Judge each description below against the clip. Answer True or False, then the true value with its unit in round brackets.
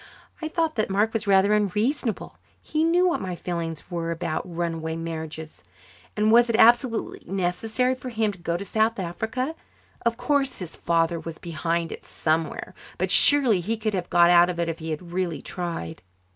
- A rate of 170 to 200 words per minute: True (185 wpm)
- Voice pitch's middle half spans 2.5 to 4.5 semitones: False (5.2 semitones)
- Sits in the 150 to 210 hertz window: True (185 Hz)